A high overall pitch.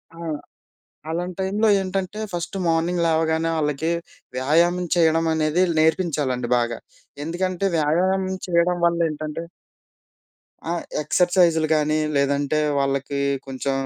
No: medium, 165 Hz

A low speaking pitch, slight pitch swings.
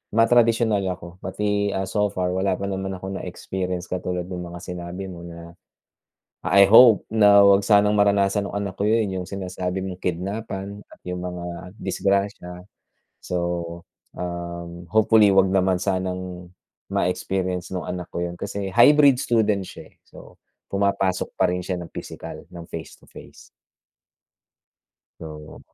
Yes: very low, 95 Hz; narrow, 2.2 semitones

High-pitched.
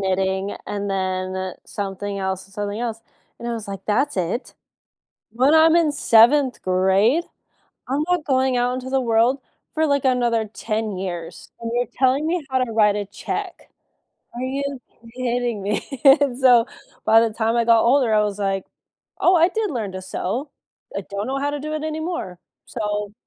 Yes: high, 230 Hz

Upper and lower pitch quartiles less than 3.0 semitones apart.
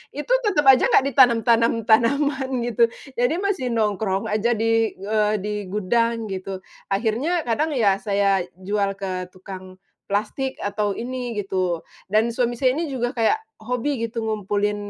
No: average, 3.7 semitones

